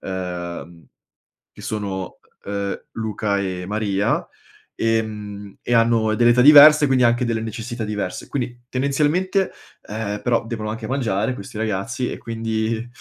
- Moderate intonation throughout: Yes, average, 3.1 semitones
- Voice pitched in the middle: No, low, 110 Hz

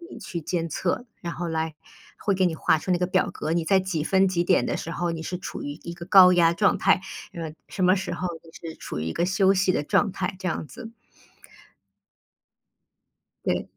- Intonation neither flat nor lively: No, narrow, 2.3 semitones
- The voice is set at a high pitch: No, medium, 180 Hz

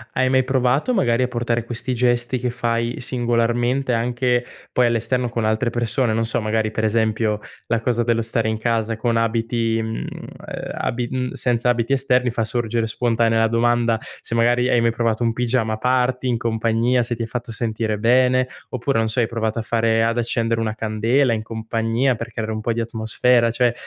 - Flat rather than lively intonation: Yes, narrow, 1.5 semitones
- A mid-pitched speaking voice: No, low, 115 Hz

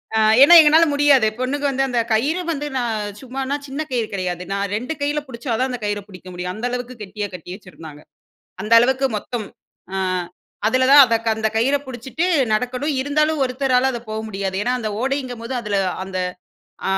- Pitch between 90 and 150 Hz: No, high, 245 Hz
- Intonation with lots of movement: No, average, 4.3 semitones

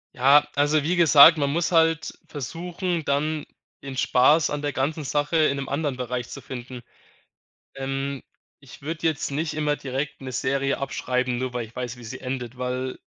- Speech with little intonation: No, average, 3.0 semitones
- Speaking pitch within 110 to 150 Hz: Yes, medium, 140 Hz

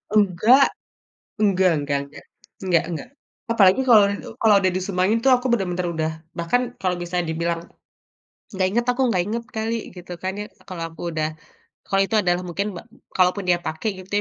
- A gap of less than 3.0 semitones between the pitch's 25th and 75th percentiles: No, average, 3.6 semitones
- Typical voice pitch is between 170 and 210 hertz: Yes, medium, 185 Hz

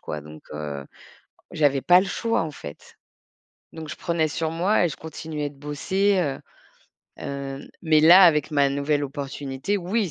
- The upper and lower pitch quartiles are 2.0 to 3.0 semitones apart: No, average, 3.7 semitones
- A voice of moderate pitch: Yes, medium, 150 Hz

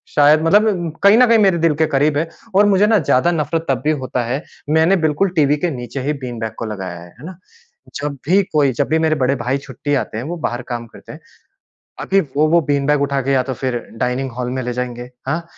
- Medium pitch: Yes, medium, 145 Hz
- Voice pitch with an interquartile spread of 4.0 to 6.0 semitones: Yes, average, 4.6 semitones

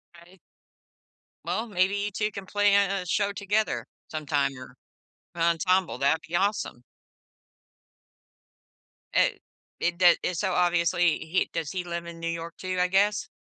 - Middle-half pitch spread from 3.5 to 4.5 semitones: No, average, 3.1 semitones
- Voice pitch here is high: No, medium, 180 Hz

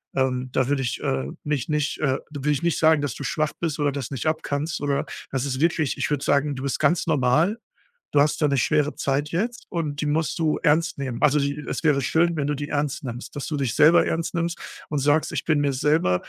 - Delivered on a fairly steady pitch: Yes, narrow, 2.3 semitones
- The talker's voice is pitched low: No, medium, 145 Hz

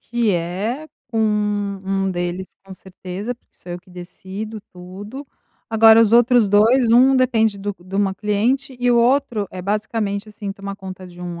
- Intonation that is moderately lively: Yes, average, 3.3 semitones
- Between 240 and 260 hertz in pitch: No, high, 205 Hz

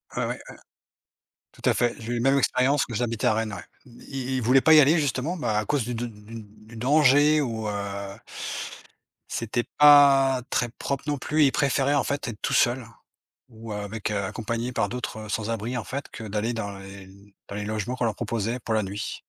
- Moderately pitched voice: No, low, 120 Hz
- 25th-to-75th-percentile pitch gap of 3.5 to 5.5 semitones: Yes, average, 3.8 semitones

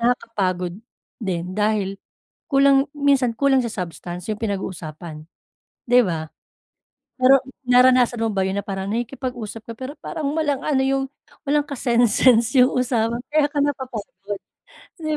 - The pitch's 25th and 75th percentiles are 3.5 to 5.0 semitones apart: No, wide, 5.4 semitones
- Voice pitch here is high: Yes, high, 240 Hz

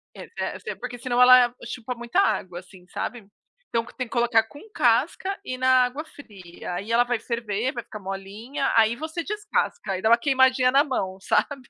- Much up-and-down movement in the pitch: No, average, 3.1 semitones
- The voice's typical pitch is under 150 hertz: No, high, 240 Hz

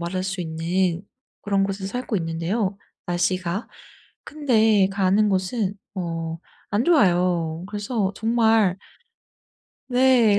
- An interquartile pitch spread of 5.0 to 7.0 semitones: No, average, 3.8 semitones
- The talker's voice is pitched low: No, high, 195 Hz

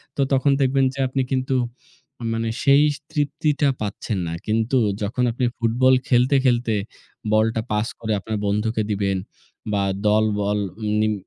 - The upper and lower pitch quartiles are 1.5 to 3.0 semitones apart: No, average, 3.7 semitones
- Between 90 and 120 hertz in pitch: Yes, low, 115 Hz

